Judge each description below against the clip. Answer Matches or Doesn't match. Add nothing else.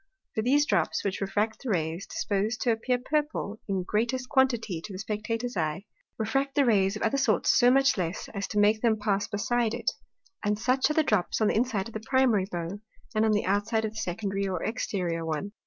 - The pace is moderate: Doesn't match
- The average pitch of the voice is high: Matches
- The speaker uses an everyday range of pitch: Matches